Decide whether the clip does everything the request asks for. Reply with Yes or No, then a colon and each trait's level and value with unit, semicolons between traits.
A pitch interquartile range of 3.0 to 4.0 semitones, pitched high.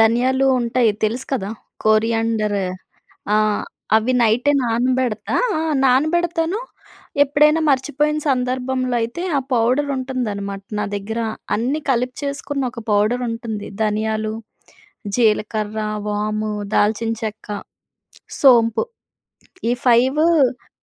Yes: average, 3.4 semitones; high, 240 Hz